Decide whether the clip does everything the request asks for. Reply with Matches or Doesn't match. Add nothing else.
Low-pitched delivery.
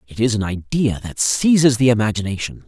Matches